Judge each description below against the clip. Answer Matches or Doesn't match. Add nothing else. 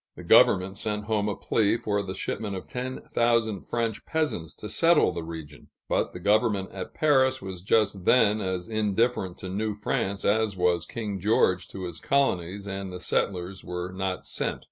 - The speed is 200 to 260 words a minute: Doesn't match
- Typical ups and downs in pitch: Matches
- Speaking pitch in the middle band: Doesn't match